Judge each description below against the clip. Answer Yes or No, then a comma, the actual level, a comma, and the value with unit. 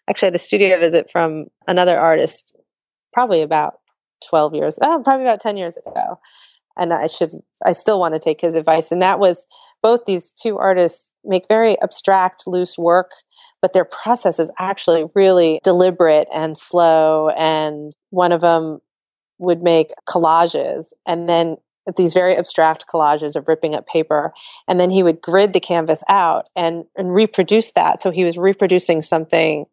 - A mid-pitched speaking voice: Yes, medium, 175 Hz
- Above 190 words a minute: No, average, 165 wpm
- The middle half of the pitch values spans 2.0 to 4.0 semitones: Yes, average, 2.8 semitones